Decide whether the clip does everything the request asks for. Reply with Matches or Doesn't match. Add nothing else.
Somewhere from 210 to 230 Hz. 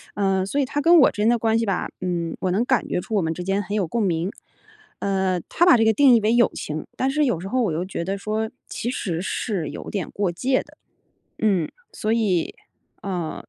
Doesn't match